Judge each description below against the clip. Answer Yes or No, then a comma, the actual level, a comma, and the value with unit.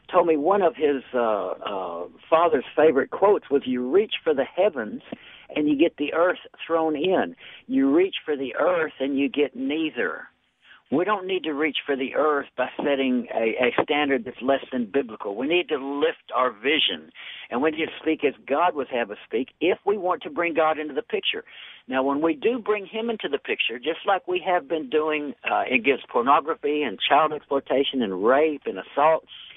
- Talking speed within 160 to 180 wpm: No, fast, 205 wpm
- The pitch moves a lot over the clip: Yes, wide, 6.0 semitones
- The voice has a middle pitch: Yes, medium, 155 Hz